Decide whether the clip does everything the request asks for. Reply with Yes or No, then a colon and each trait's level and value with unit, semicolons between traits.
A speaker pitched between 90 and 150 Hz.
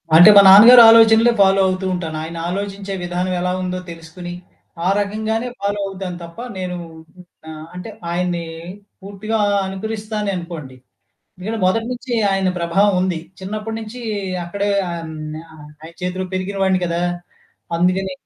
No: high, 190 Hz